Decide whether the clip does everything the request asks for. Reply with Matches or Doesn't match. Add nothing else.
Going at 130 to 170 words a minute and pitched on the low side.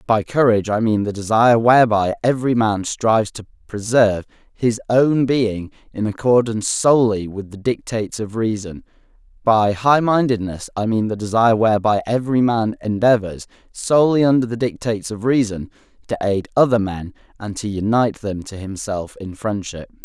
Matches